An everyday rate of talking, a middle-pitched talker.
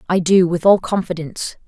Yes: average, 180 wpm; medium, 175 Hz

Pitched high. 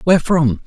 No: medium, 155 Hz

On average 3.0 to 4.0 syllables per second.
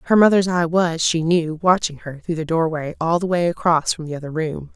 No: 5.4 syllables/s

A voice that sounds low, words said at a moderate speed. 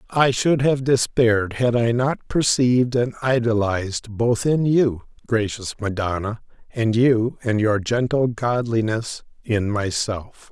No: low, 115 Hz; slow, 130 wpm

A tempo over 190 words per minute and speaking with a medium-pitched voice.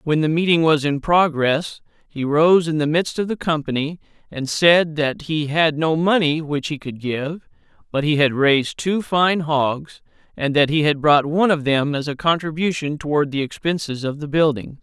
Yes: average, 200 wpm; medium, 155 Hz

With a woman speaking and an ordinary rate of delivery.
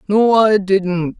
No: male; average, 150 wpm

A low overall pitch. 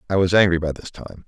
Yes: very low, 90 Hz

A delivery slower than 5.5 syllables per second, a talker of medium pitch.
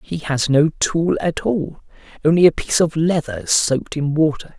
Yes: 4.7 syllables/s; medium, 155 Hz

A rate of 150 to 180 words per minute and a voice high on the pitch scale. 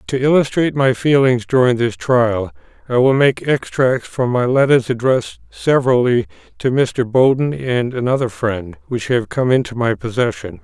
No: average, 160 wpm; low, 125 Hz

